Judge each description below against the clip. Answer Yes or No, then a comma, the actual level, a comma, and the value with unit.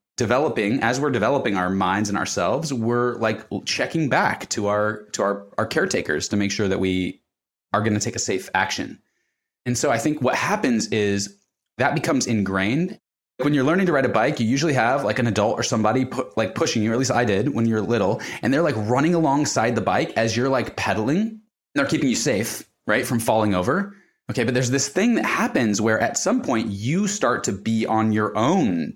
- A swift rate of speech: Yes, fast, 220 wpm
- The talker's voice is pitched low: Yes, low, 115 Hz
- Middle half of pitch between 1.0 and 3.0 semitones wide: No, average, 4.5 semitones